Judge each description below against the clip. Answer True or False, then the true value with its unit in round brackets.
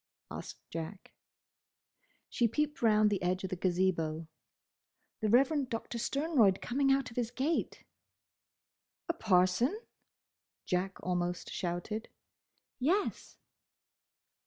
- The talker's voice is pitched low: False (215 Hz)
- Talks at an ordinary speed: False (105 wpm)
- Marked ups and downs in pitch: True (6.6 semitones)